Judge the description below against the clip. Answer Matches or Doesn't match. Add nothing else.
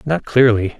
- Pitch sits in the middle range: Doesn't match